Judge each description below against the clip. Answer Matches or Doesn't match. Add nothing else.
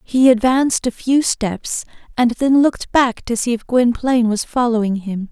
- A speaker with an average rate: Matches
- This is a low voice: Doesn't match